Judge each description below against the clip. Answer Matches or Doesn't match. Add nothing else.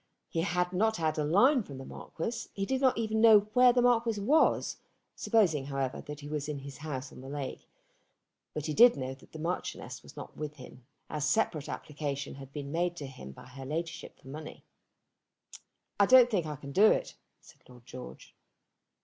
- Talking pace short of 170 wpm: Doesn't match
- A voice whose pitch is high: Doesn't match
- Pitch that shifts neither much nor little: Doesn't match